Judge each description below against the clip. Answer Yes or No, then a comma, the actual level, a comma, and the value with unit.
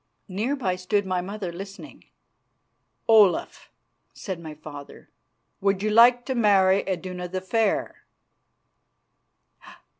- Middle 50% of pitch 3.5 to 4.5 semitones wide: No, average, 2.8 semitones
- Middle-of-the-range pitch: No, high, 195 Hz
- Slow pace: Yes, slow, 110 wpm